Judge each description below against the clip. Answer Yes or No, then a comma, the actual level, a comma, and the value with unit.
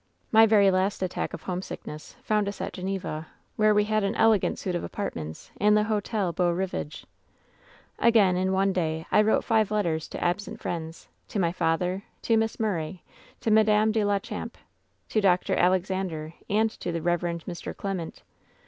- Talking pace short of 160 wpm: No, average, 180 wpm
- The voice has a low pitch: No, high, 190 Hz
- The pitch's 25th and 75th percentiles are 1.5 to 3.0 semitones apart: No, average, 3.4 semitones